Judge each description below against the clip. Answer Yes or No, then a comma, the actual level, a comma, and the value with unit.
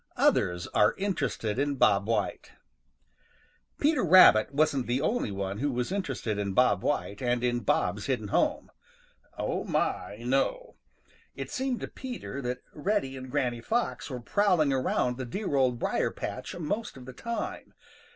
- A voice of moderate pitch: No, low, 130 Hz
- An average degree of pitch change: No, wide, 7.4 semitones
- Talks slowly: No, average, 155 wpm